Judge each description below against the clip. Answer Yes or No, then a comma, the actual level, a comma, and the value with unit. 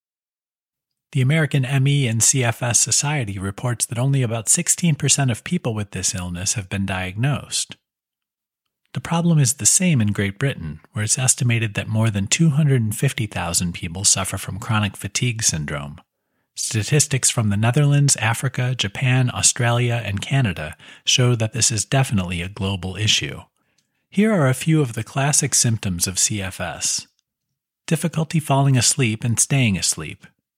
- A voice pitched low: Yes, low, 120 Hz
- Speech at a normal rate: Yes, average, 145 wpm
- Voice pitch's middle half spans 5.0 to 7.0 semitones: Yes, wide, 5.6 semitones